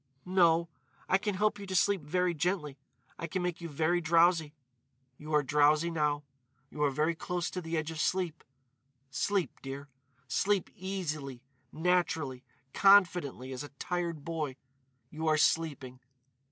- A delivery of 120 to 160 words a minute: Yes, average, 150 wpm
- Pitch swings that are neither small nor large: Yes, average, 3.3 semitones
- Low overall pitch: No, medium, 165 Hz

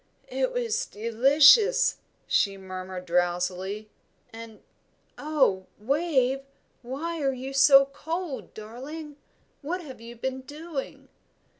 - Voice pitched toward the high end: Yes, very high, 265 Hz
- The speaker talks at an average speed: No, slow, 105 wpm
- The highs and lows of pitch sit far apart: Yes, wide, 6.3 semitones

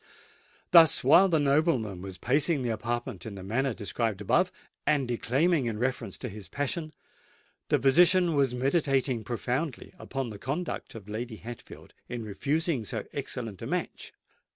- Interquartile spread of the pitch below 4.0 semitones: No, average, 4.7 semitones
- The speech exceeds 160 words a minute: No, average, 155 wpm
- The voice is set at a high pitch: No, low, 125 Hz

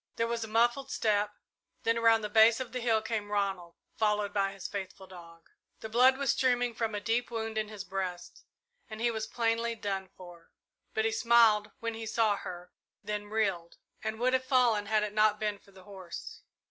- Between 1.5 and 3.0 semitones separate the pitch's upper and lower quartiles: Yes, narrow, 2.4 semitones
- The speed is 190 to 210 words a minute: Yes, average, 200 wpm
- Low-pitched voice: No, high, 215 Hz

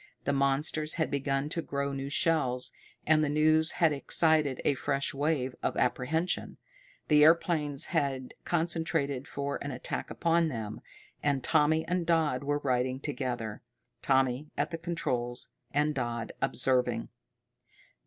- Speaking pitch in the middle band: Yes, medium, 145 Hz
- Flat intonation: No, average, 3.3 semitones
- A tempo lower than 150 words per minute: Yes, slow, 135 wpm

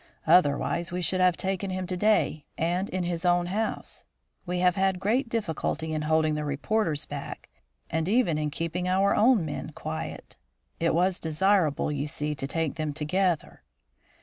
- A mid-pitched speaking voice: Yes, medium, 175 Hz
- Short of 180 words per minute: Yes, average, 170 wpm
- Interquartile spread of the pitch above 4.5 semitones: No, average, 3.4 semitones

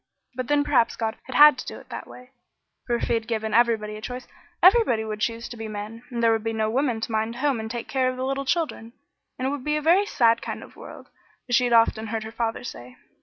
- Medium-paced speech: No, fast, 265 wpm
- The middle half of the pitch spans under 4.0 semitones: Yes, average, 2.8 semitones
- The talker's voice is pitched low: No, high, 235 Hz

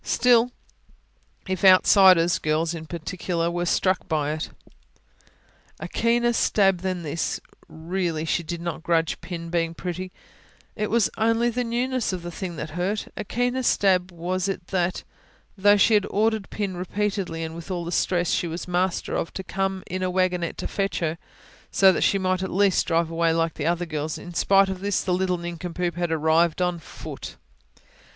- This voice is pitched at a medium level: Yes, medium, 180 Hz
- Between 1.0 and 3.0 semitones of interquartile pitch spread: Yes, narrow, 2.6 semitones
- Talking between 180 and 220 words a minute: Yes, average, 185 wpm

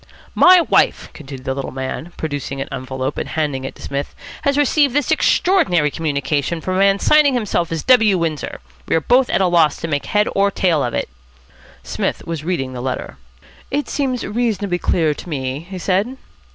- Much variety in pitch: Yes, wide, 7.0 semitones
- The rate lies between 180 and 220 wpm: Yes, average, 190 wpm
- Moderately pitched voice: Yes, medium, 170 Hz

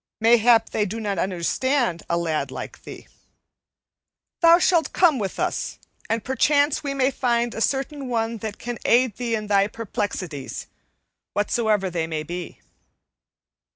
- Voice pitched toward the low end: No, high, 225 Hz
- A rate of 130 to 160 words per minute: Yes, average, 145 wpm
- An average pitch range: Yes, average, 4.8 semitones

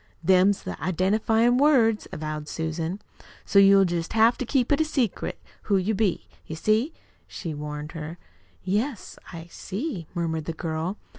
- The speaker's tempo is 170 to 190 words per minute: No, average, 150 wpm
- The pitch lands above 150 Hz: Yes, high, 190 Hz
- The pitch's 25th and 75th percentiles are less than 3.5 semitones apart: No, wide, 5.4 semitones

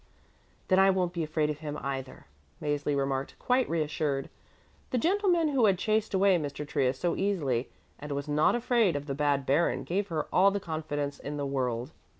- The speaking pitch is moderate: Yes, medium, 150 Hz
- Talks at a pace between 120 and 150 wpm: No, average, 185 wpm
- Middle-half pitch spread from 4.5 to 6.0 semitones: Yes, wide, 5.5 semitones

